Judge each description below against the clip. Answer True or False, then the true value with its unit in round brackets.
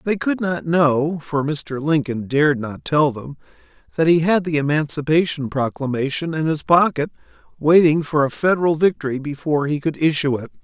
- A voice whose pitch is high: False (150 Hz)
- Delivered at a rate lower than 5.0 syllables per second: False (5.2 syllables/s)